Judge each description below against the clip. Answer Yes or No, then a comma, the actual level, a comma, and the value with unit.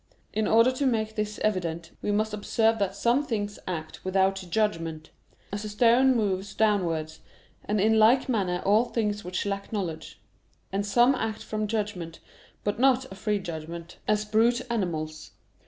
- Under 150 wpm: No, average, 160 wpm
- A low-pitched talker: No, high, 210 Hz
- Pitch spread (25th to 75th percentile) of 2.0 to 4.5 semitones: Yes, average, 3.2 semitones